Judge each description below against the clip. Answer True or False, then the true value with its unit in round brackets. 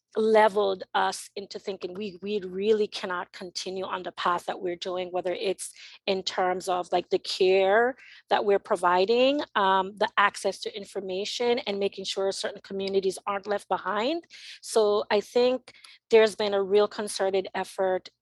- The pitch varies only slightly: True (2.0 semitones)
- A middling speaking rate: True (160 wpm)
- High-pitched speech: True (200 Hz)